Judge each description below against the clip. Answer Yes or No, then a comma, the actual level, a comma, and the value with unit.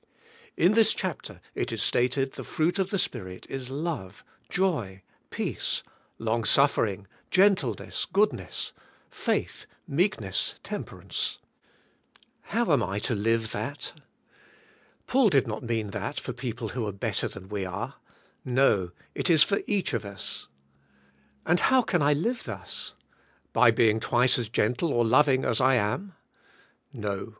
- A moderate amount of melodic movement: No, wide, 7.3 semitones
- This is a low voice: Yes, low, 125 Hz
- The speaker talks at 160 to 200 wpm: No, average, 140 wpm